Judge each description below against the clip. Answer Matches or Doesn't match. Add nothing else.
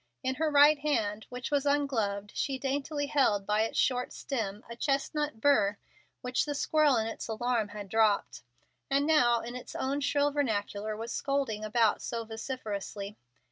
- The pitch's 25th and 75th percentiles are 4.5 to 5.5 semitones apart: Matches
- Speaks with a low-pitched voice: Doesn't match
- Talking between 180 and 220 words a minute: Doesn't match